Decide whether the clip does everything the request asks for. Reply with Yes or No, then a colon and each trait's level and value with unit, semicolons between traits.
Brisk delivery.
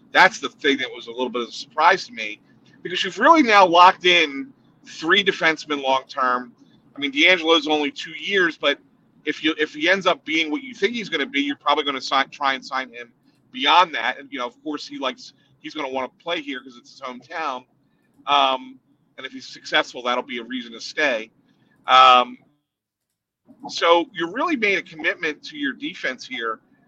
Yes: fast, 210 wpm